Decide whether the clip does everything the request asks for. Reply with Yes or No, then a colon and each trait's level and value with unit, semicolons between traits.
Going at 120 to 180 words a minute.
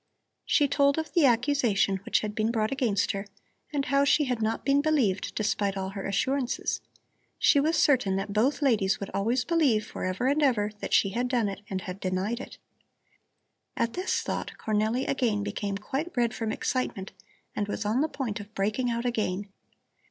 No: average, 190 wpm